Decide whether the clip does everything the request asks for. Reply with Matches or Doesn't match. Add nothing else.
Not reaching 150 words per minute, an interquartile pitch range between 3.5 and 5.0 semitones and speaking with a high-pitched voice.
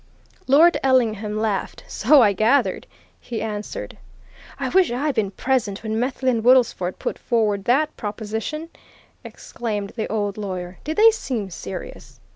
Matches